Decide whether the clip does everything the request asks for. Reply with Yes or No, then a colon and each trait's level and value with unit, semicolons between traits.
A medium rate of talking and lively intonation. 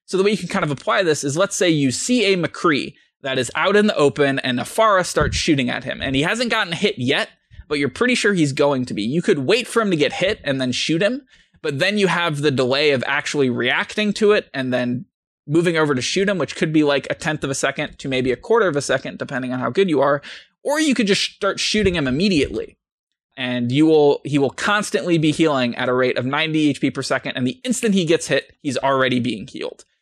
No: fast, 255 wpm; wide, 6.8 semitones